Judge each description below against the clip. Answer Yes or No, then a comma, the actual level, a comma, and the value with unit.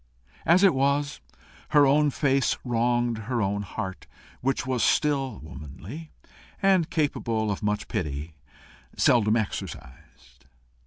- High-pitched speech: No, low, 120 Hz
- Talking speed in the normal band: No, slow, 115 wpm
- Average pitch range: No, wide, 5.9 semitones